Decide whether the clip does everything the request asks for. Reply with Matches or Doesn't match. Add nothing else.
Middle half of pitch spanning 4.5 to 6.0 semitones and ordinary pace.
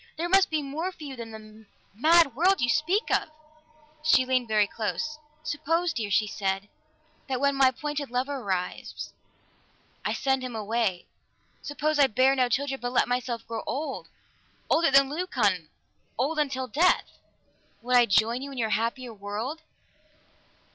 Matches